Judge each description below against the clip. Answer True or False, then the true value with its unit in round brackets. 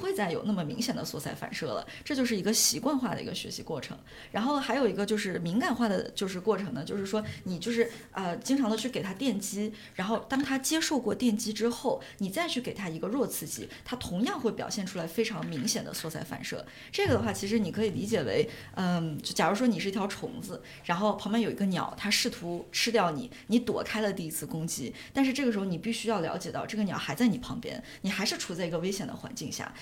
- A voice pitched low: False (215 Hz)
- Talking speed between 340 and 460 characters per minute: True (360 characters per minute)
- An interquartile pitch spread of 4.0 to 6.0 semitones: False (3.4 semitones)